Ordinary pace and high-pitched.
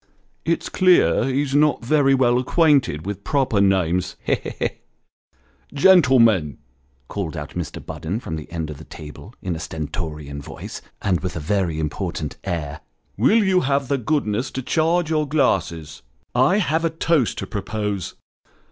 No: average, 170 wpm; low, 105 Hz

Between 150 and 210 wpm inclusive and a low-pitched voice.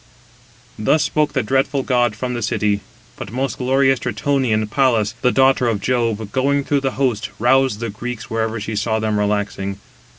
Yes: average, 170 wpm; low, 120 Hz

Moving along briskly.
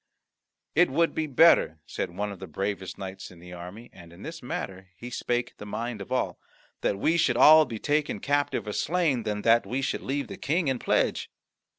Yes: fast, 210 wpm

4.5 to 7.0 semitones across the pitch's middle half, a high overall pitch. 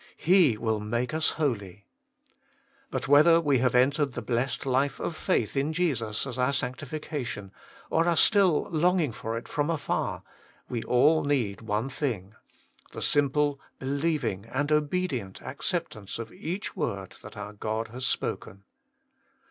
No: average, 5.2 semitones; low, 135 Hz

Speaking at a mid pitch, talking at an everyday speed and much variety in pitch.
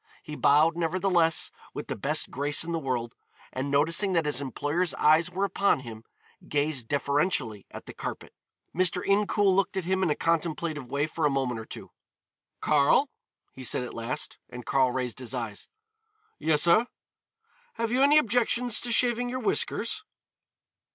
Yes: medium, 155 Hz; average, 165 wpm; wide, 6.0 semitones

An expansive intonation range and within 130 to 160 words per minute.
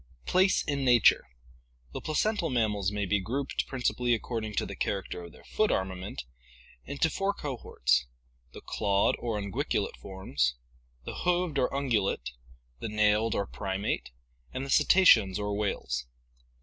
Yes: wide, 6.2 semitones; average, 150 wpm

